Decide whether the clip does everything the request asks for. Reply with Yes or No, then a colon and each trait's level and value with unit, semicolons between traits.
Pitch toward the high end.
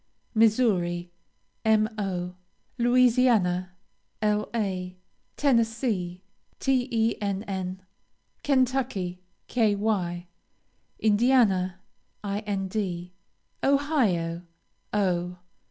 Yes: high, 205 Hz